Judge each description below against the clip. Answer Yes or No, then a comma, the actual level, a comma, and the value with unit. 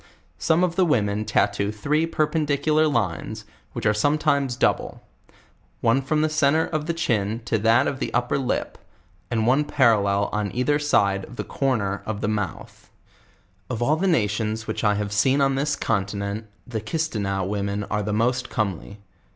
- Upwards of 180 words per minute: No, average, 175 wpm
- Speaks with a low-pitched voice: Yes, low, 115 Hz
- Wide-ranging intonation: Yes, wide, 5.9 semitones